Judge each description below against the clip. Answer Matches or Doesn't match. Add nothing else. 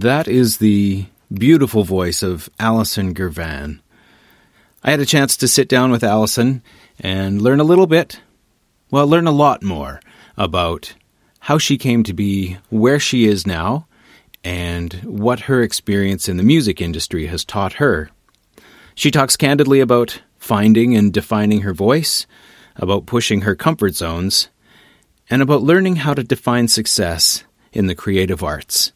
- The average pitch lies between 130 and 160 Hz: Doesn't match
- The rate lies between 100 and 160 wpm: Matches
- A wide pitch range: Matches